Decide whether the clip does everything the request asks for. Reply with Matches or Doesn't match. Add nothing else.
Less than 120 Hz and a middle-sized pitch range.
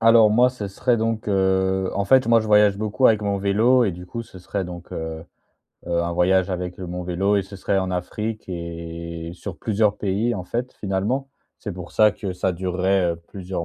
Matches